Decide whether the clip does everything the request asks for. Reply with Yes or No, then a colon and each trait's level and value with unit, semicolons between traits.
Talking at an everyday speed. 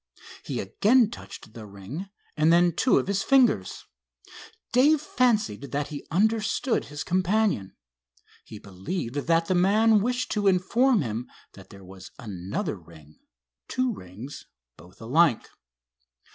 No: slow, 130 wpm